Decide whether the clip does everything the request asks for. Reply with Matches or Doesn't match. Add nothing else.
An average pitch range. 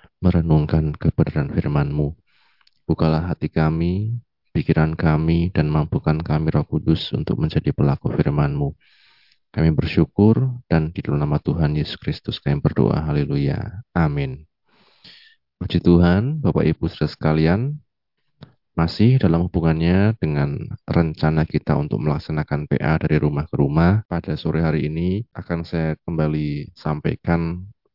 Doesn't match